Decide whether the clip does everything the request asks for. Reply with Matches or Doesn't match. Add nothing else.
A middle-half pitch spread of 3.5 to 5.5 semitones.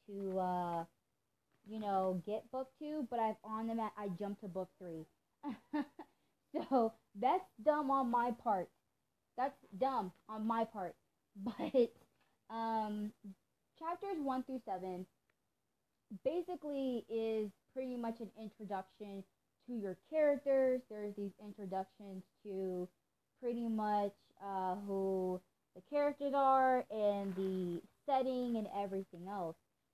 Matches